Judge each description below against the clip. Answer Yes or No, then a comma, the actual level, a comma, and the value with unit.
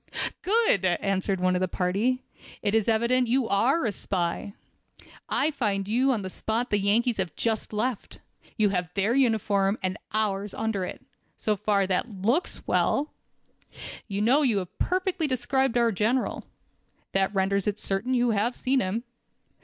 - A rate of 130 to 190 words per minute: Yes, average, 165 wpm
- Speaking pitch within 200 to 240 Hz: Yes, high, 215 Hz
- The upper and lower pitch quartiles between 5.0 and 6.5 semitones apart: No, average, 4.1 semitones